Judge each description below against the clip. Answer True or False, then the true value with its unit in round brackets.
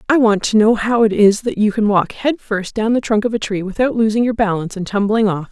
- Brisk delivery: True (285 wpm)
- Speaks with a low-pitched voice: False (215 Hz)